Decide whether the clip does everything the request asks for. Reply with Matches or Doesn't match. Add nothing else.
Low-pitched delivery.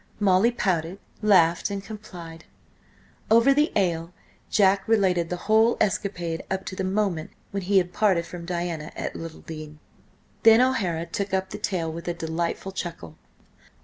Doesn't match